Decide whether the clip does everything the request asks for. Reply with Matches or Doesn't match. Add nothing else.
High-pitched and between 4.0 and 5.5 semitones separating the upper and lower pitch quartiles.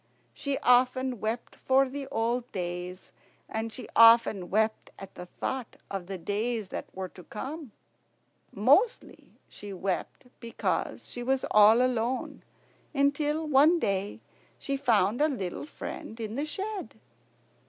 Matches